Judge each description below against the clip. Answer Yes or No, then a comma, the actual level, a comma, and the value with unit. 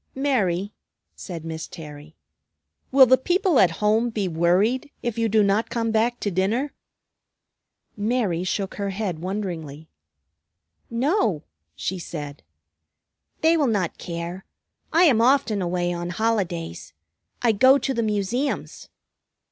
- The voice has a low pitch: No, high, 205 Hz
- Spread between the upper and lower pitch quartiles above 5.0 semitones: Yes, wide, 5.6 semitones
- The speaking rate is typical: No, slow, 130 wpm